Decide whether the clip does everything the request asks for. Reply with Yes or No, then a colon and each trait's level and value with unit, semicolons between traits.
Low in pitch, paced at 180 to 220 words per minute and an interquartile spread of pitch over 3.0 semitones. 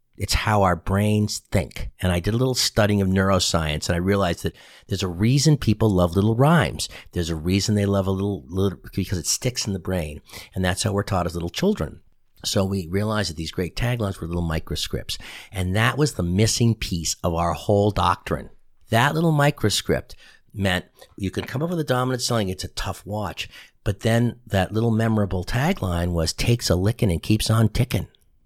Yes: low, 100 Hz; average, 200 wpm; average, 3.8 semitones